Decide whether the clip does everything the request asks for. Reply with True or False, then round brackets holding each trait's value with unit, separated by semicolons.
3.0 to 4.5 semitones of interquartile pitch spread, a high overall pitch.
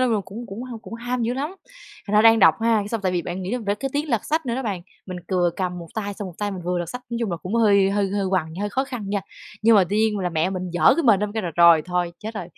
True (4.1 semitones; 205 Hz)